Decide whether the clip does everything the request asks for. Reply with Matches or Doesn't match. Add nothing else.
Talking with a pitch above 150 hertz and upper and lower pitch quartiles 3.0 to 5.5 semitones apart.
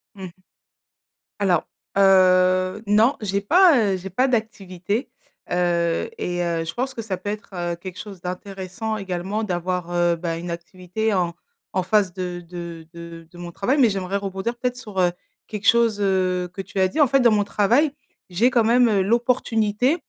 Matches